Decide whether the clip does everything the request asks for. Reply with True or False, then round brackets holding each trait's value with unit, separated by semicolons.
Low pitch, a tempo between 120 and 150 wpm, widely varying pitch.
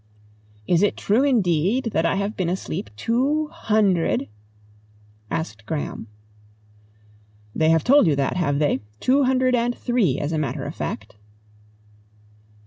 False (185 Hz; 140 wpm; 8.4 semitones)